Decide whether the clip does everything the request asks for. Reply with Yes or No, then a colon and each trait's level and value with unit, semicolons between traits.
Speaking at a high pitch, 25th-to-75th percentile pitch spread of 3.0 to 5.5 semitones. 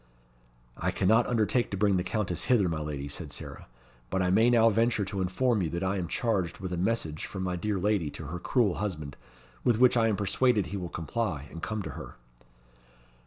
No: very low, 95 Hz; average, 4.3 semitones